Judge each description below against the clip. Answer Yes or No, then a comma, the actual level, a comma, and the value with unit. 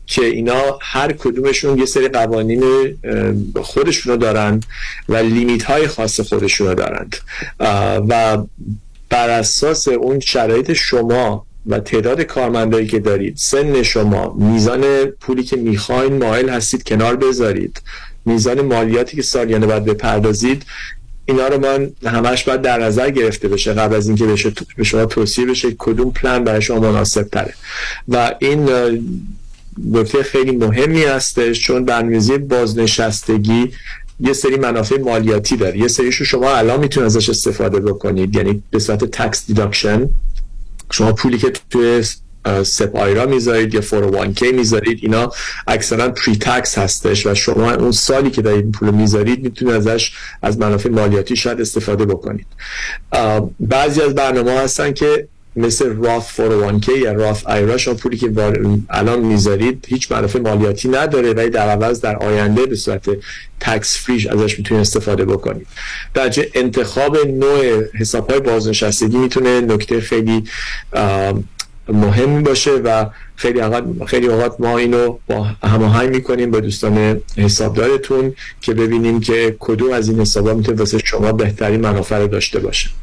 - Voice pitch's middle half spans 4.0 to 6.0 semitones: No, average, 2.8 semitones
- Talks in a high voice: No, low, 115 Hz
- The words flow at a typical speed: Yes, average, 140 wpm